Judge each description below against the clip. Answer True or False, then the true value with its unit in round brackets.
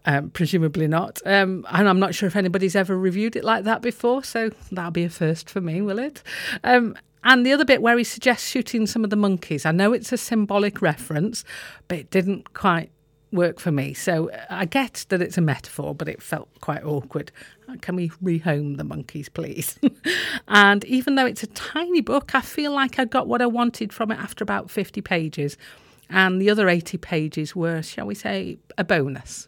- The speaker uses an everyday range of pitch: False (5.7 semitones)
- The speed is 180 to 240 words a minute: True (205 wpm)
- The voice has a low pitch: False (195 Hz)